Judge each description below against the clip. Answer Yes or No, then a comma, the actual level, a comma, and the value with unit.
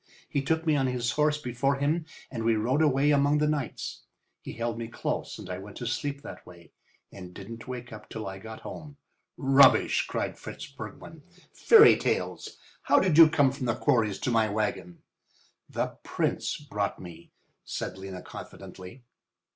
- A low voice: Yes, low, 125 Hz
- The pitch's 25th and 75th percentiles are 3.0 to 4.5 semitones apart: No, average, 5.2 semitones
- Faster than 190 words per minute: No, average, 175 wpm